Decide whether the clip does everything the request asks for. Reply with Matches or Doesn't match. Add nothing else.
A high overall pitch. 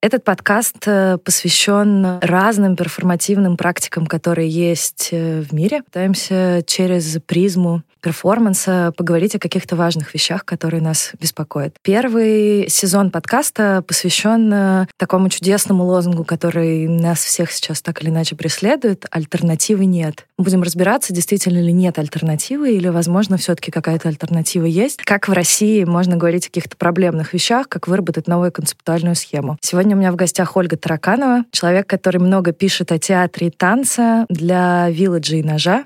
Doesn't match